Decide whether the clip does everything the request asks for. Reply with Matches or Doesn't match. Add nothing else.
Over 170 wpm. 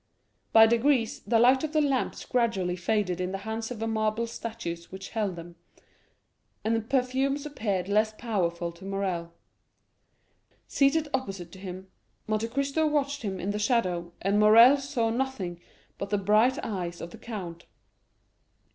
Doesn't match